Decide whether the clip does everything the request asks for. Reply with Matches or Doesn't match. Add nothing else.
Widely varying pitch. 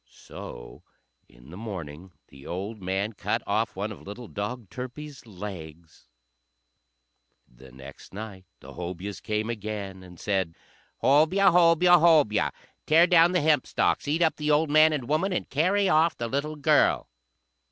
Matches